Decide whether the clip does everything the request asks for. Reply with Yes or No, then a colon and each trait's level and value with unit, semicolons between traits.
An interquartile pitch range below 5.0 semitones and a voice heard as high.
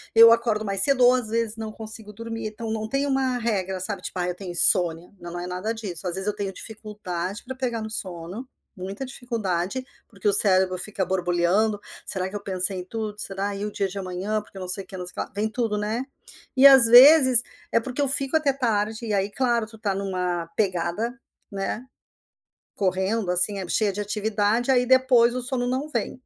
Yes: average, 3.7 semitones; high, 210 Hz